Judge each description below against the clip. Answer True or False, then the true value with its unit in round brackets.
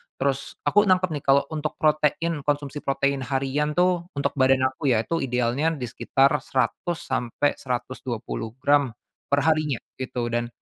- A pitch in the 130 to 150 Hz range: True (140 Hz)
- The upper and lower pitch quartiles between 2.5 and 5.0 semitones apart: True (2.9 semitones)